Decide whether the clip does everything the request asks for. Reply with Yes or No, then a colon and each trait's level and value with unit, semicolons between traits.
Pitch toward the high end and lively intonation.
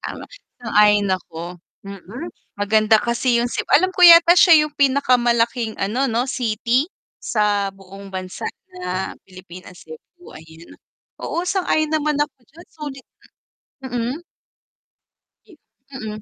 Yes: high, 235 Hz; wide, 6.6 semitones